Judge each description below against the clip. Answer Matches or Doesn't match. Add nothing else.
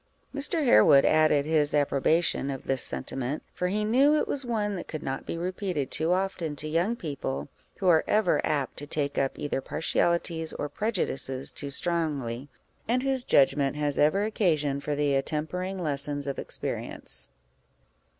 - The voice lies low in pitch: Doesn't match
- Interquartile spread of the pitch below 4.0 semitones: Doesn't match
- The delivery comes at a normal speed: Matches